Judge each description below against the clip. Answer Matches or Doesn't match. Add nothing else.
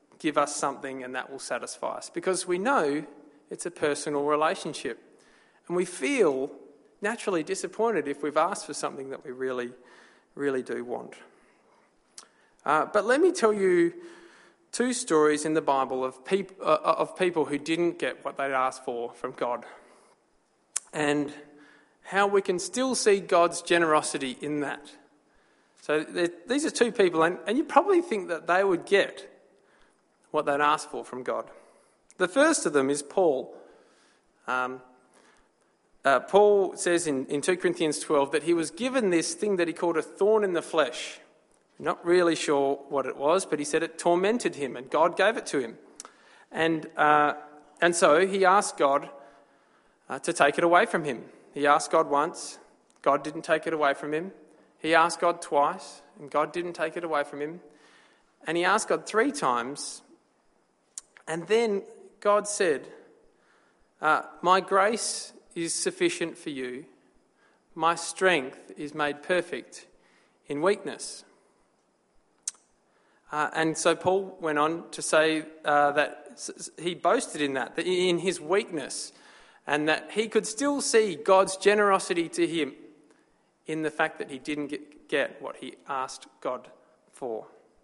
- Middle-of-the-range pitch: Matches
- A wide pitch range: Doesn't match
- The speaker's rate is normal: Matches